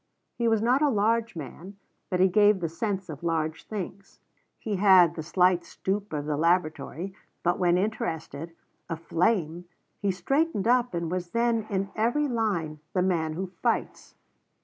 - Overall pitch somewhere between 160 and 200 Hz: Yes, medium, 185 Hz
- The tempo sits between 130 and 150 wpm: No, average, 160 wpm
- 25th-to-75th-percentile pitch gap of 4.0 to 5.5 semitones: Yes, average, 4.3 semitones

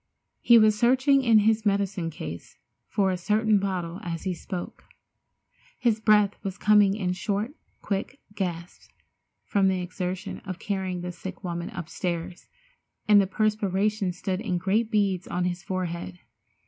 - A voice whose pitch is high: Yes, high, 195 Hz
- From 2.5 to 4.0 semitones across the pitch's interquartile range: Yes, average, 2.9 semitones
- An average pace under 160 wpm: Yes, average, 150 wpm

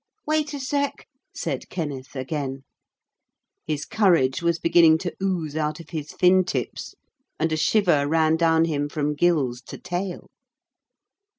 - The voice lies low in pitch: No, medium, 160 Hz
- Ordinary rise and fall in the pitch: Yes, average, 3.5 semitones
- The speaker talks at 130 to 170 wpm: Yes, average, 140 wpm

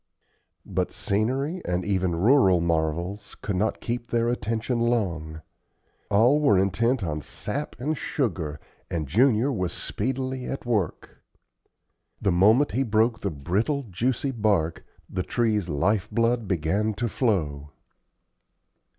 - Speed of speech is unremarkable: No, slow, 125 wpm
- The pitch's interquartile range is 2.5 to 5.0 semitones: No, wide, 5.4 semitones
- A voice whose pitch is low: Yes, low, 105 Hz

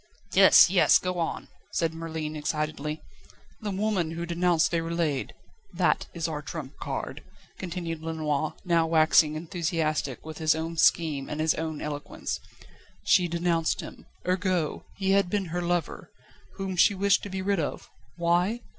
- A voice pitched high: No, medium, 165 Hz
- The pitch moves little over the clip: Yes, narrow, 2.3 semitones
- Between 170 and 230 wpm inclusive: No, average, 150 wpm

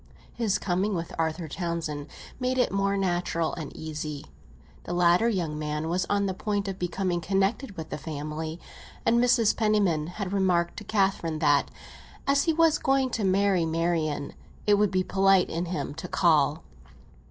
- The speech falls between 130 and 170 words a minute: Yes, average, 165 wpm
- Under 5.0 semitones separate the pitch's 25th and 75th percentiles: Yes, average, 3.9 semitones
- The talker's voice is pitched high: No, medium, 180 Hz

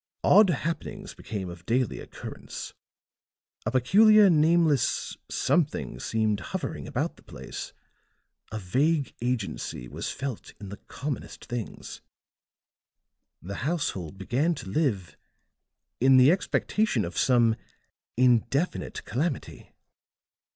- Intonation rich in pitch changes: Yes, wide, 6.8 semitones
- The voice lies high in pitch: No, low, 130 Hz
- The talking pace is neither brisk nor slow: No, slow, 105 wpm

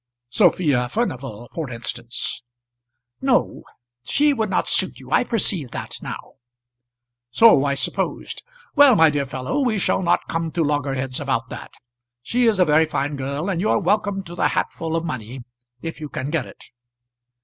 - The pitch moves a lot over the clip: Yes, wide, 6.7 semitones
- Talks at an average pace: Yes, average, 170 wpm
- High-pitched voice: No, medium, 155 Hz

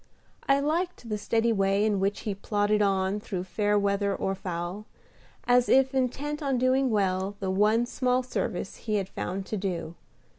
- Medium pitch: No, high, 210 Hz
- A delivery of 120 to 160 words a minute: No, average, 175 wpm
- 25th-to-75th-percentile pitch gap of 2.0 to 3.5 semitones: No, average, 4.3 semitones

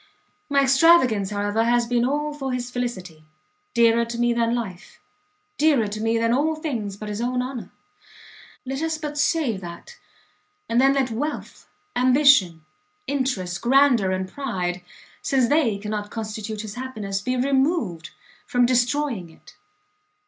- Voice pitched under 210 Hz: No, high, 240 Hz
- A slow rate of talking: No, average, 145 wpm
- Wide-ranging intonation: No, average, 4.5 semitones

